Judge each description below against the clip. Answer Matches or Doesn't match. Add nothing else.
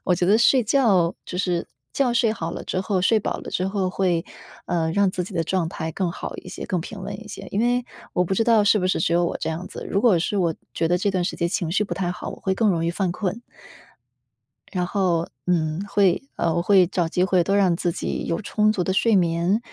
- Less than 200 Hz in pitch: Matches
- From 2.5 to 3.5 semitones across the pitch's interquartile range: Matches